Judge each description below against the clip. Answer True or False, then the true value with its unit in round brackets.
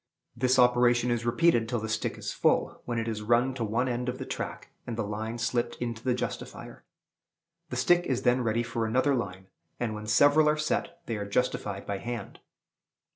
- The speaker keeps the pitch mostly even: True (2.1 semitones)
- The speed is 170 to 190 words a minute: False (200 wpm)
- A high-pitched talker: False (120 Hz)